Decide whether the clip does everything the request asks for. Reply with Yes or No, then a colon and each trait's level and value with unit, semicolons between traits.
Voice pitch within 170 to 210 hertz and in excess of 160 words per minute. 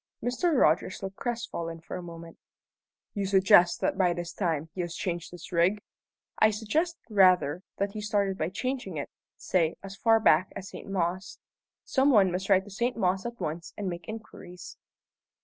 Yes: high, 190 Hz; average, 180 wpm